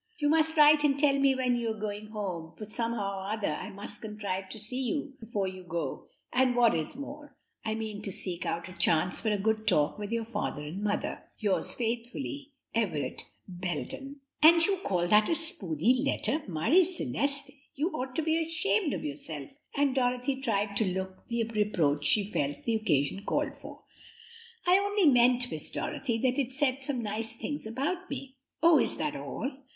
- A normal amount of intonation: No, wide, 6.0 semitones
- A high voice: Yes, high, 230 Hz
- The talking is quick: No, average, 190 wpm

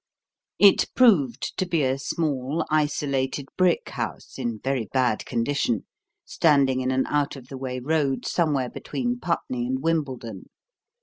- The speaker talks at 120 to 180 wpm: Yes, average, 140 wpm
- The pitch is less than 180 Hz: Yes, low, 135 Hz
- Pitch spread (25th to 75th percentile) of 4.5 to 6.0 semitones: No, average, 3.4 semitones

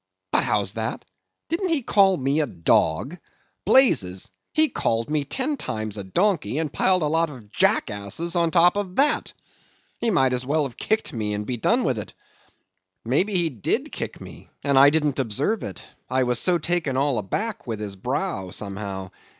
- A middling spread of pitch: No, wide, 8.8 semitones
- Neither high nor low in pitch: Yes, medium, 145 Hz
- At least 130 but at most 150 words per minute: No, average, 180 wpm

